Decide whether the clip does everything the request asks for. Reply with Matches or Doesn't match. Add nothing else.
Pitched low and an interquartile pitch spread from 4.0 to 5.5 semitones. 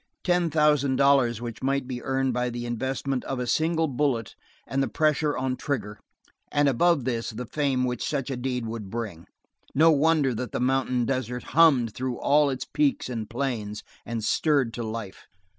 Doesn't match